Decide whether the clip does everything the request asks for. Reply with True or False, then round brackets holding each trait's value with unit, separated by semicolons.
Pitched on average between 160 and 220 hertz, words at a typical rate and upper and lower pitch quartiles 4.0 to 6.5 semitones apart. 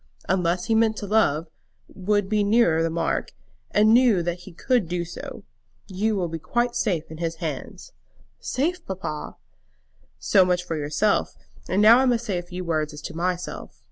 True (185 Hz; 180 wpm; 4.5 semitones)